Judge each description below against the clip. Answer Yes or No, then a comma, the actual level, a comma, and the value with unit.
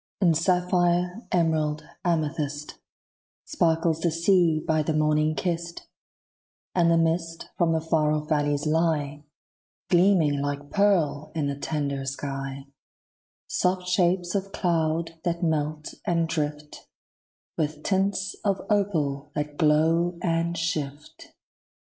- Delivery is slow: Yes, slow, 115 wpm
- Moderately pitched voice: Yes, medium, 160 Hz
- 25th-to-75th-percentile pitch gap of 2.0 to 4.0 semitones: Yes, narrow, 2.5 semitones